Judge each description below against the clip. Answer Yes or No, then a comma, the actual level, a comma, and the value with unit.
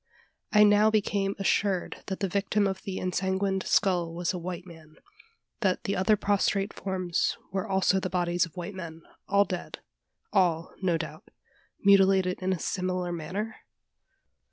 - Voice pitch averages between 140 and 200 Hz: Yes, high, 190 Hz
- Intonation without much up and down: Yes, narrow, 2.0 semitones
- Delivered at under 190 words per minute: Yes, average, 155 wpm